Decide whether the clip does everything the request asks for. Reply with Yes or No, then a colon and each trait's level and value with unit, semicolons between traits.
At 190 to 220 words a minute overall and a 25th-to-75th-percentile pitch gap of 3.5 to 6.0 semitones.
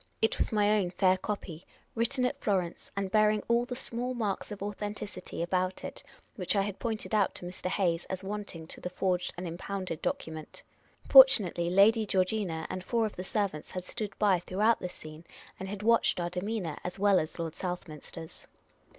No: average, 200 wpm; average, 3.0 semitones